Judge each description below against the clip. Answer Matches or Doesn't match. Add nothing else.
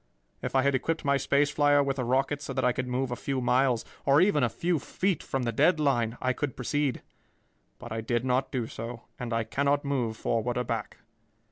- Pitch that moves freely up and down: Doesn't match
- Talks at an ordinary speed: Doesn't match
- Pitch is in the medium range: Doesn't match